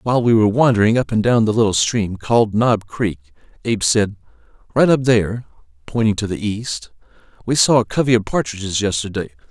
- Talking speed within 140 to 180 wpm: Yes, average, 170 wpm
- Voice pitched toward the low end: Yes, low, 110 Hz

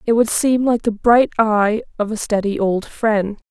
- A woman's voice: Yes, female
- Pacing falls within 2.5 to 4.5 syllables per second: Yes, 4.3 syllables/s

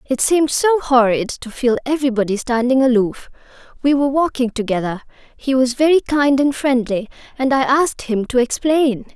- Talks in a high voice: Yes, very high, 260 Hz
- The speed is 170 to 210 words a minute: No, average, 145 wpm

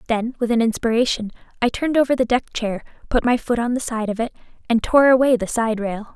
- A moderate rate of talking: No, fast, 235 wpm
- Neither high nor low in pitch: No, high, 235 Hz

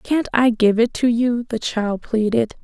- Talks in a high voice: Yes, high, 225 Hz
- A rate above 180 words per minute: Yes, fast, 205 wpm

